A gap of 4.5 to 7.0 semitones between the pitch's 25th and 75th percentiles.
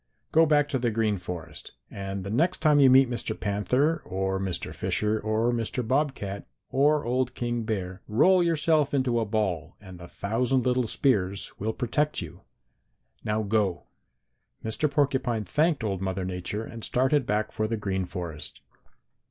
Yes: average, 5.3 semitones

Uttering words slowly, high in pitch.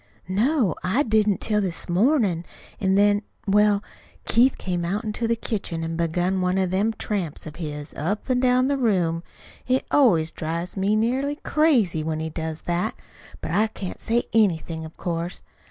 No: average, 170 wpm; high, 195 Hz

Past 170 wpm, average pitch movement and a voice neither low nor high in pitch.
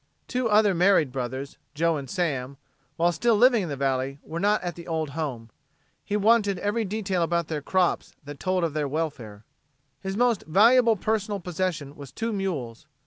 No: average, 180 wpm; wide, 6.2 semitones; medium, 175 Hz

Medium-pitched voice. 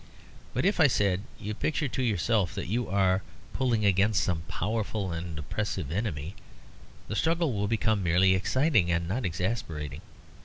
No: low, 100 Hz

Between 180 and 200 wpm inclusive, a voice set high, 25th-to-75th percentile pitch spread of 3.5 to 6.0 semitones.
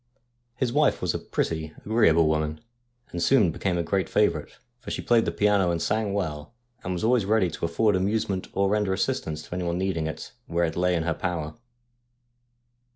No: average, 190 wpm; very low, 90 Hz; average, 4.0 semitones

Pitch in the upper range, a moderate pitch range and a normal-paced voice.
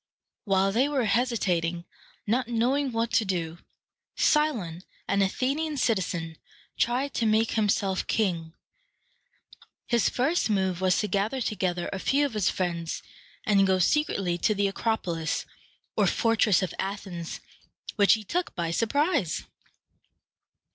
No: high, 205 Hz; average, 4.7 semitones; slow, 130 wpm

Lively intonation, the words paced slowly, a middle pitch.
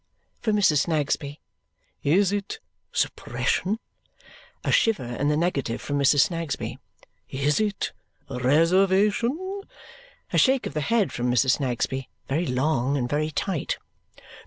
Yes: wide, 6.5 semitones; slow, 125 wpm; medium, 155 Hz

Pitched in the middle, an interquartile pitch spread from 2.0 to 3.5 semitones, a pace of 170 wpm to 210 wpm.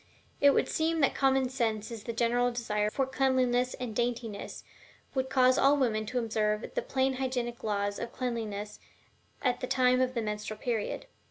No: high, 245 Hz; average, 3.1 semitones; average, 175 wpm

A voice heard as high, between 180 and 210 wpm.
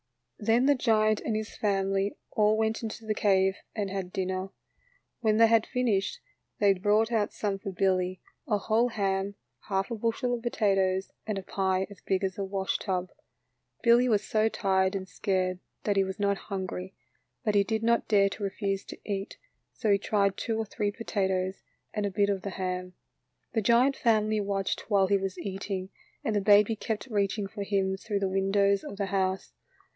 Yes: high, 200 Hz; average, 190 wpm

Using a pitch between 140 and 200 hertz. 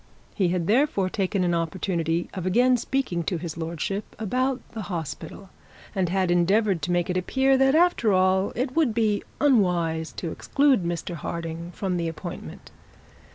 Yes: medium, 185 Hz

